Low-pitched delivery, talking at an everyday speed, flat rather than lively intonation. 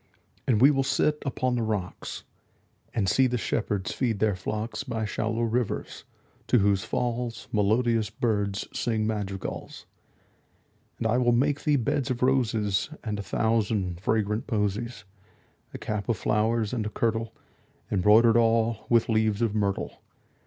Yes: low, 110 Hz; average, 150 wpm; narrow, 2.3 semitones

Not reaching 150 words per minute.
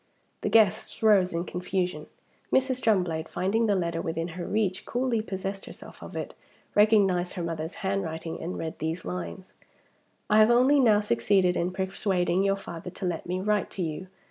No: average, 170 wpm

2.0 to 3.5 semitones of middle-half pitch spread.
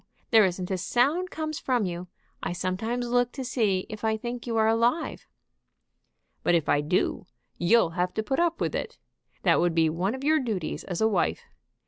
No: average, 5.3 semitones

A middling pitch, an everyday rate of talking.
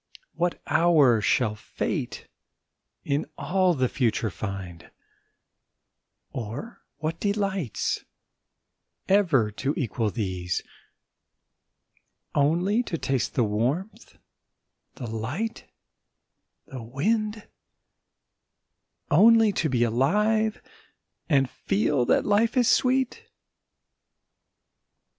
No: medium, 145 Hz; slow, 85 wpm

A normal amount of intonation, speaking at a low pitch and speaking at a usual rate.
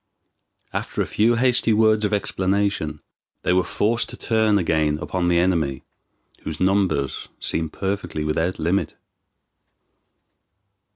No: average, 4.8 semitones; very low, 95 Hz; slow, 120 wpm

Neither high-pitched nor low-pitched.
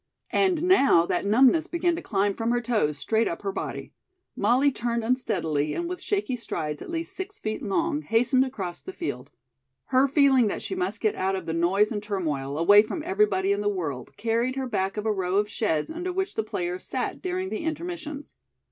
No: high, 225 Hz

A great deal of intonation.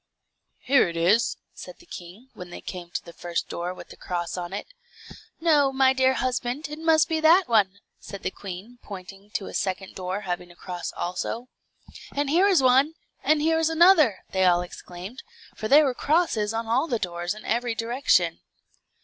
Yes: wide, 7.5 semitones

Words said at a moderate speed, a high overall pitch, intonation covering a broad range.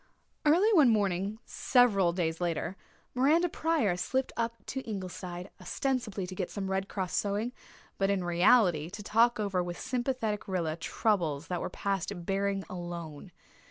No: average, 150 wpm; high, 195 Hz; average, 4.7 semitones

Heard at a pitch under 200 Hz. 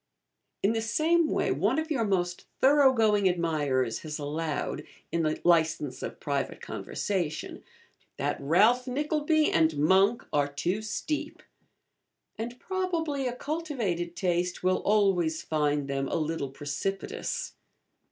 Yes: medium, 185 Hz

